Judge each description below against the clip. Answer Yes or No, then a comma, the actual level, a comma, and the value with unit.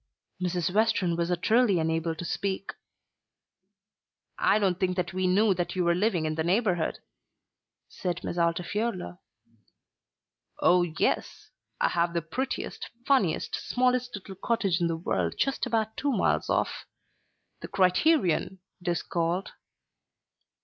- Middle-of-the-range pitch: Yes, medium, 180 Hz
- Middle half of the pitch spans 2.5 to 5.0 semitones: Yes, average, 3.9 semitones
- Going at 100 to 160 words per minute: Yes, slow, 135 wpm